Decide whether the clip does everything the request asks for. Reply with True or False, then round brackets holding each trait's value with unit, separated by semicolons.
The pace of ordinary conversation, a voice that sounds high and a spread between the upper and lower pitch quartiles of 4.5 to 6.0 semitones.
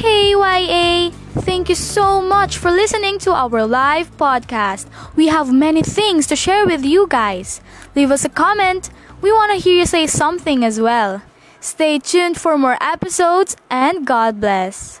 True (170 wpm; 335 Hz; 5.4 semitones)